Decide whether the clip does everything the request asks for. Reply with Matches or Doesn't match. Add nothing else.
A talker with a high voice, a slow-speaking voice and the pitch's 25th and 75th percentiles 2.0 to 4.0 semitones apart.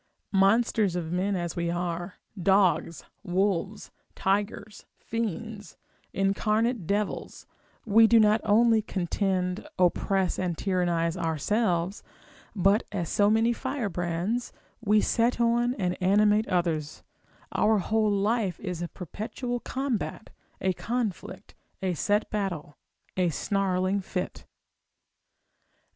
Matches